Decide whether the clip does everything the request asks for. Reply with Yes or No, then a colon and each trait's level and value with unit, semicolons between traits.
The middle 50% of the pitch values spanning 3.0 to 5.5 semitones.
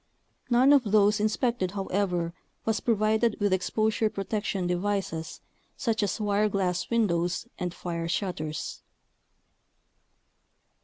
Yes: average, 3.4 semitones